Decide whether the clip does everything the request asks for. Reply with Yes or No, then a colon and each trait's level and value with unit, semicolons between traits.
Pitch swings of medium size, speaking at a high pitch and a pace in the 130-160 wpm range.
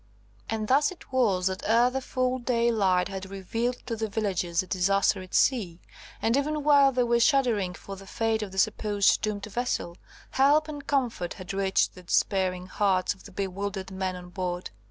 No: average, 4.6 semitones; high, 205 Hz; average, 185 wpm